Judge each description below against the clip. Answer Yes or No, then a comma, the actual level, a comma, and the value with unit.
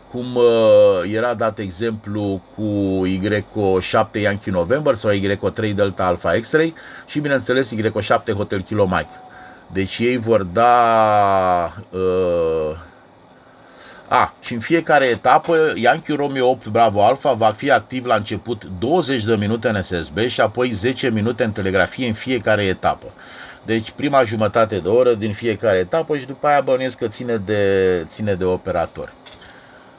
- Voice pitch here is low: Yes, low, 115 Hz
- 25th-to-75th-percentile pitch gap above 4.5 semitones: No, average, 4.0 semitones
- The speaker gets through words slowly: No, average, 140 wpm